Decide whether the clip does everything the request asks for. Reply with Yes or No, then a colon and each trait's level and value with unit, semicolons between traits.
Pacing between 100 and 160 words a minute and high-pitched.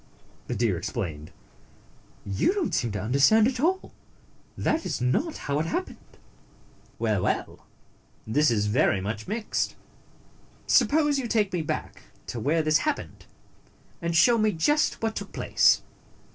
No: average, 145 wpm; medium, 165 Hz